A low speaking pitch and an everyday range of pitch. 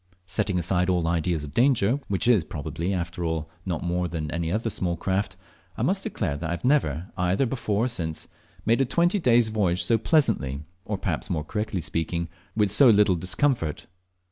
Yes: very low, 90 Hz; average, 5.0 semitones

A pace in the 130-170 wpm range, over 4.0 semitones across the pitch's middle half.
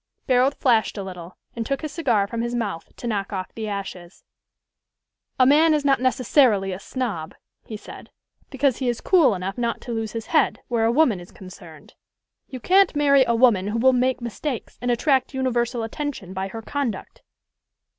No: average, 185 wpm; average, 4.7 semitones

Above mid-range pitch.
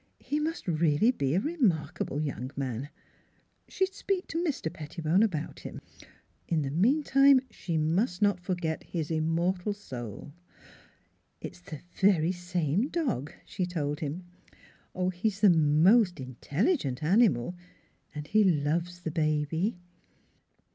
No: medium, 175 Hz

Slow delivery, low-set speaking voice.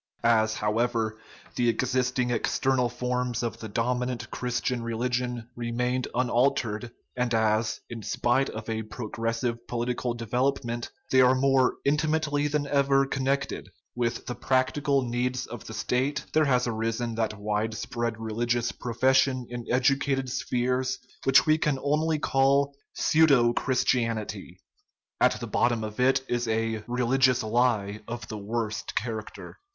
No: average, 145 wpm; low, 125 Hz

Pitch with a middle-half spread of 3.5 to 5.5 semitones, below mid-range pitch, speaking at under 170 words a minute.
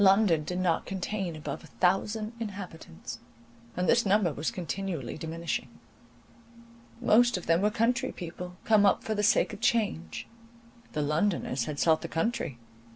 No: average, 4.7 semitones; medium, 180 Hz; average, 155 wpm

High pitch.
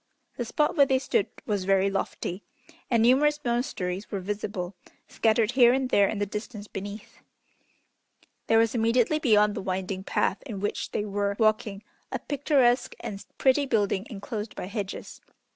Yes: high, 215 Hz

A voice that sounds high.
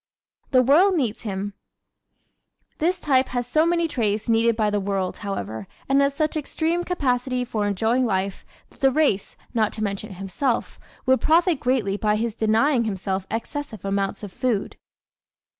Yes: high, 230 Hz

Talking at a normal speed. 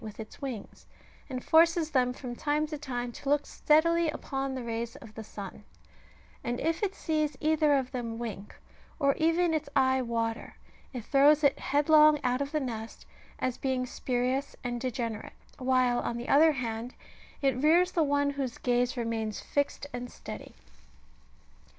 Yes: average, 170 wpm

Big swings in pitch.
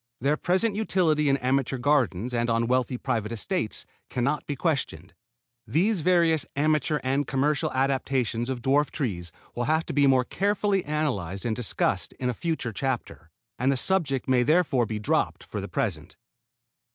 No: average, 4.4 semitones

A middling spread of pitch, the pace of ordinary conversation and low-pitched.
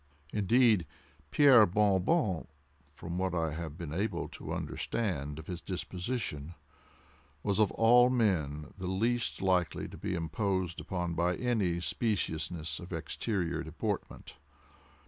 No: average, 4.4 semitones; slow, 125 wpm; very low, 90 Hz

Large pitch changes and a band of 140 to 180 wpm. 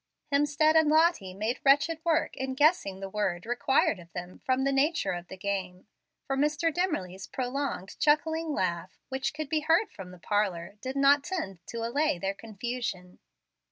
Yes: wide, 7.9 semitones; average, 170 wpm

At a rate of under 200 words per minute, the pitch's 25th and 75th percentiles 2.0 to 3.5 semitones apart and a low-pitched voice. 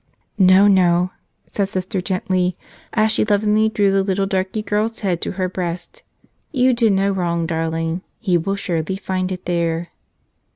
No: average, 160 wpm; average, 2.7 semitones; high, 190 Hz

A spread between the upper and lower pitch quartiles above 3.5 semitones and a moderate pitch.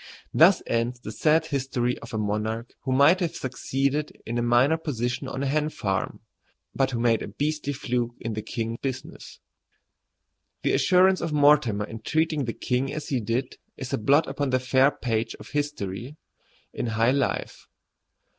No: average, 3.9 semitones; low, 130 Hz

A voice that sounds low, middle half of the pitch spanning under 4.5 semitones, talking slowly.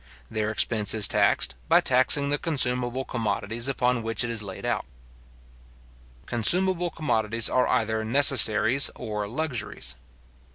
Yes: low, 120 Hz; average, 3.4 semitones; slow, 125 wpm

